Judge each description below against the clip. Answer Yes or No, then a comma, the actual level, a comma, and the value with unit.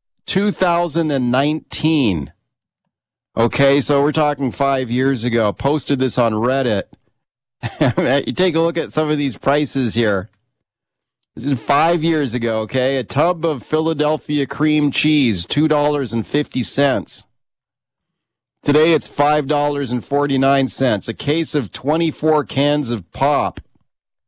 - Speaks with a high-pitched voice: No, medium, 140 Hz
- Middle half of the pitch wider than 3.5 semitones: No, average, 3.2 semitones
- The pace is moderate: No, slow, 110 wpm